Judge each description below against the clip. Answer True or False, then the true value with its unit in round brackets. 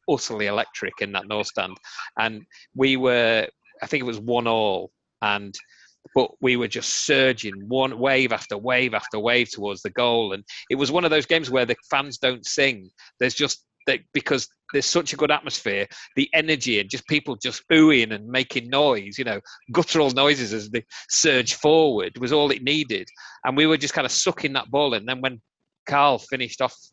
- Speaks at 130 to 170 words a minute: False (195 wpm)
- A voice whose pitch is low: True (130 Hz)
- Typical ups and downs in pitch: True (3.9 semitones)